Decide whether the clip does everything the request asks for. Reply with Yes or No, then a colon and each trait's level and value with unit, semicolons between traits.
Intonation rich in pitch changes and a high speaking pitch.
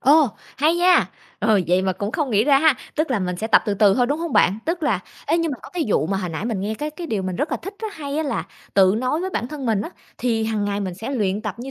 Yes: wide, 7.1 semitones; high, 230 Hz